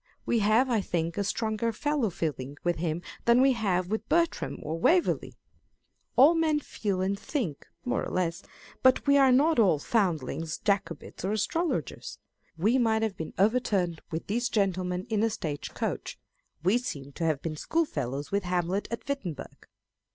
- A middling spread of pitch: No, wide, 6.2 semitones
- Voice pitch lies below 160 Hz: No, high, 200 Hz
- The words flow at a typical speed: Yes, average, 165 wpm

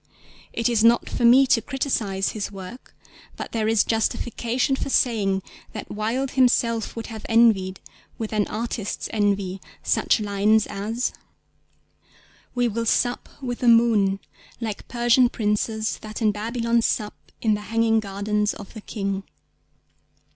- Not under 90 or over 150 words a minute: Yes, average, 140 wpm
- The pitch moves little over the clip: Yes, narrow, 2.3 semitones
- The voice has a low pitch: No, high, 225 Hz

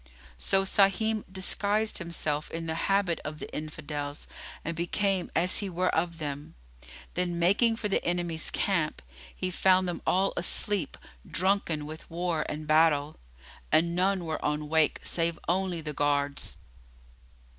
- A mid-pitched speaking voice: Yes, medium, 170 Hz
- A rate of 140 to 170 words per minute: Yes, average, 145 wpm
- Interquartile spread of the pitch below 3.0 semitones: No, average, 3.5 semitones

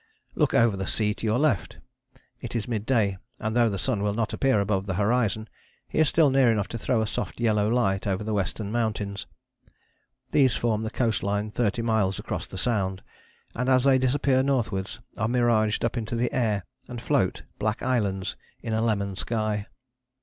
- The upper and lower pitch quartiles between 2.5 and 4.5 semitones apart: Yes, average, 2.9 semitones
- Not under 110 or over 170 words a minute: No, average, 195 wpm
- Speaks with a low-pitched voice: Yes, low, 110 Hz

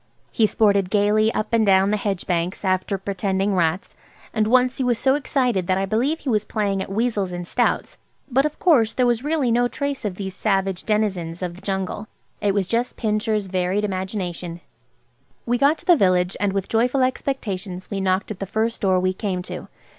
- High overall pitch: Yes, high, 205 Hz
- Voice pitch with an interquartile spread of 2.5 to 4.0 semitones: Yes, average, 3.7 semitones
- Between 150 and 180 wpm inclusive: No, average, 200 wpm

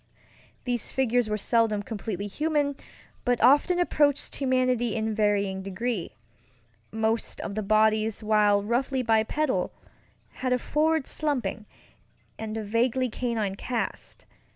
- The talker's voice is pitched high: Yes, high, 230 Hz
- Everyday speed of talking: No, slow, 120 wpm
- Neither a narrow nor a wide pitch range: Yes, average, 3.2 semitones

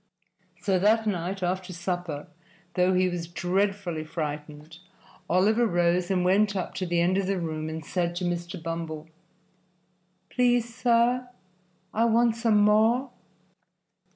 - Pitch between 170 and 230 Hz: Yes, medium, 185 Hz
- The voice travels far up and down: No, average, 3.7 semitones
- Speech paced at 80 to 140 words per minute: Yes, slow, 135 wpm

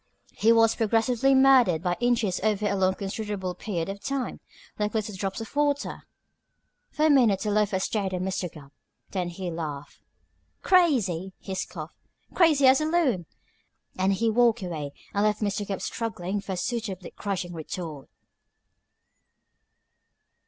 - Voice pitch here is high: Yes, high, 205 Hz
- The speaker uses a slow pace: No, average, 150 wpm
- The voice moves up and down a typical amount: Yes, average, 4.1 semitones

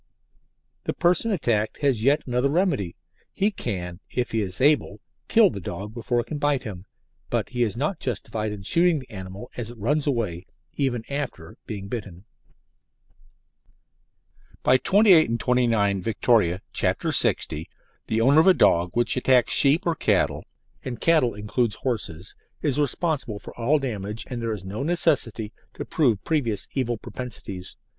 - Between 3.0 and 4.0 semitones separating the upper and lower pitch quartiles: No, wide, 5.6 semitones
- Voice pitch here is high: No, low, 120 Hz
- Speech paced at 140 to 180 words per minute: Yes, average, 160 wpm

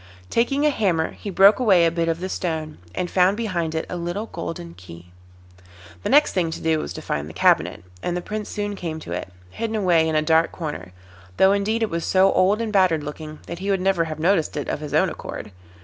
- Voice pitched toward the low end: No, medium, 175 Hz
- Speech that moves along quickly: Yes, fast, 235 wpm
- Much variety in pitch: No, average, 4.0 semitones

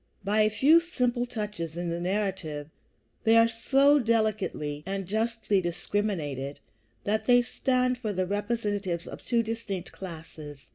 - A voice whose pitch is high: Yes, high, 205 Hz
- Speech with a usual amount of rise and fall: Yes, average, 4.9 semitones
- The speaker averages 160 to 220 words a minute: No, average, 140 wpm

